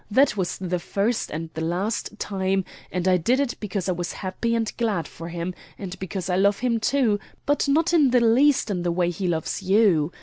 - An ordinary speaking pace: No, fast, 215 wpm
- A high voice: Yes, high, 195 Hz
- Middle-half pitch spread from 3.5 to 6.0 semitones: Yes, average, 4.7 semitones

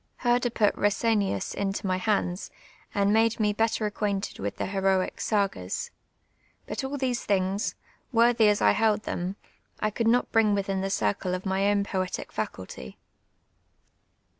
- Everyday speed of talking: Yes, average, 150 wpm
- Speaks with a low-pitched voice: No, high, 205 Hz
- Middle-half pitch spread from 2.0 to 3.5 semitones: Yes, average, 2.8 semitones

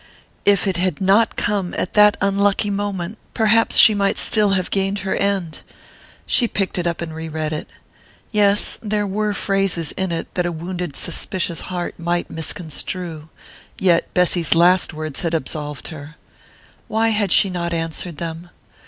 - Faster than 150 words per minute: Yes, average, 160 wpm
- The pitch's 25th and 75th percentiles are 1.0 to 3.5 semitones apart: Yes, average, 3.2 semitones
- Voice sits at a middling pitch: Yes, medium, 180 Hz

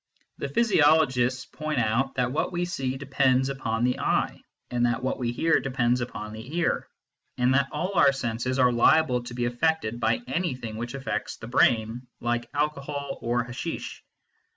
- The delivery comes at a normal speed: Yes, average, 165 wpm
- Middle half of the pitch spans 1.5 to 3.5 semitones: Yes, average, 3.0 semitones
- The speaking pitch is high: No, low, 130 Hz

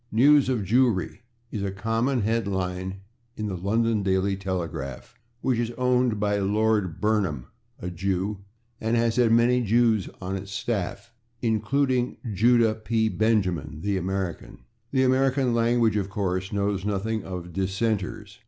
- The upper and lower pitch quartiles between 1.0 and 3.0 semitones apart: No, average, 3.5 semitones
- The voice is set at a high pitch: No, low, 105 Hz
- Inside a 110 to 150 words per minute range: Yes, average, 145 wpm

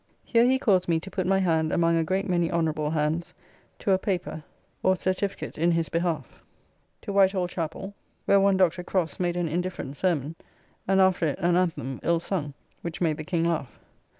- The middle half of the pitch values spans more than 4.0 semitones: No, narrow, 2.6 semitones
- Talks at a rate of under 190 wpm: No, average, 195 wpm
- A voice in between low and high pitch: Yes, medium, 175 Hz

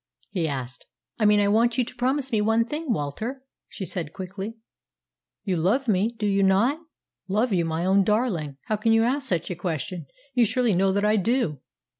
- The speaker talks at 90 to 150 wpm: No, average, 200 wpm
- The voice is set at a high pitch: Yes, high, 205 Hz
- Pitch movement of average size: Yes, average, 4.5 semitones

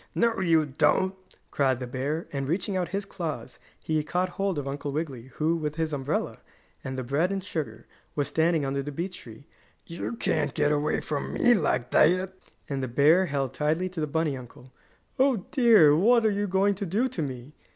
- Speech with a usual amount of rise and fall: Yes, average, 4.9 semitones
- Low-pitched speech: No, medium, 155 Hz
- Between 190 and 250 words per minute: Yes, average, 200 wpm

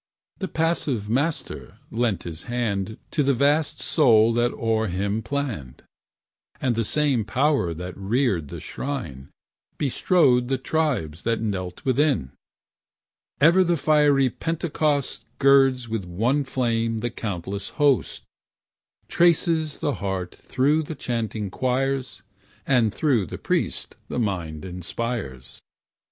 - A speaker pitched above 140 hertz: No, low, 120 Hz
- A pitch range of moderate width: No, wide, 6.0 semitones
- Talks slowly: Yes, slow, 120 wpm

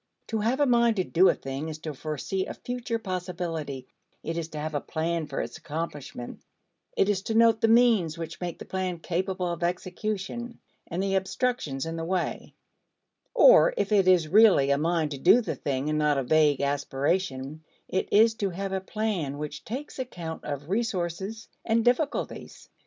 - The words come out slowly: No, average, 185 wpm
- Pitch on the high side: No, medium, 180 Hz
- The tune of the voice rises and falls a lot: Yes, wide, 5.9 semitones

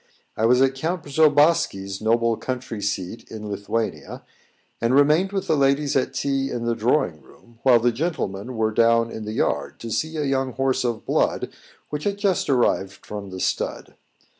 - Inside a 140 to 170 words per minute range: No, average, 180 wpm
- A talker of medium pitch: No, low, 125 Hz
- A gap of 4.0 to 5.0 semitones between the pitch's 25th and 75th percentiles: Yes, average, 4.3 semitones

